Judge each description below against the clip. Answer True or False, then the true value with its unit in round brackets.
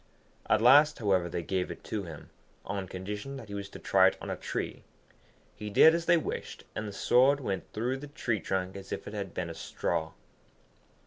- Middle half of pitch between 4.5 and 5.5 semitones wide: True (5.1 semitones)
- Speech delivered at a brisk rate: True (210 wpm)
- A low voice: True (105 Hz)